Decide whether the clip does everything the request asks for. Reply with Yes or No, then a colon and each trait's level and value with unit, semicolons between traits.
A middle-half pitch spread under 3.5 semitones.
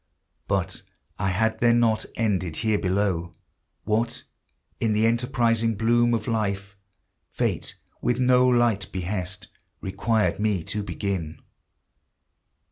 Yes: average, 3.1 semitones